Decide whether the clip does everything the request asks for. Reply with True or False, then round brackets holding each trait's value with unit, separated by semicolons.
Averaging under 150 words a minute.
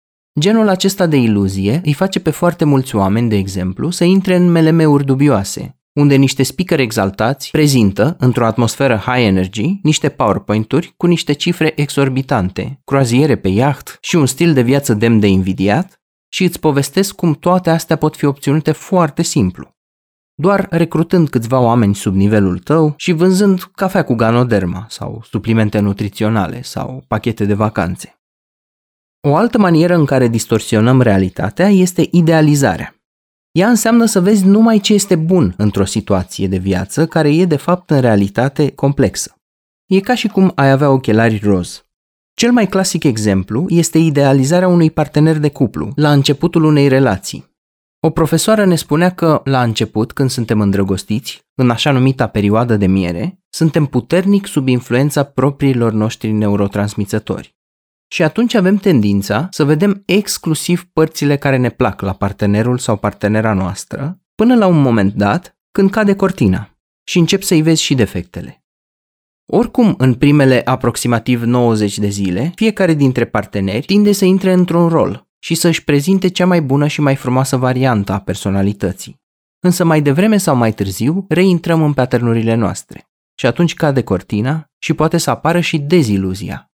False (155 wpm)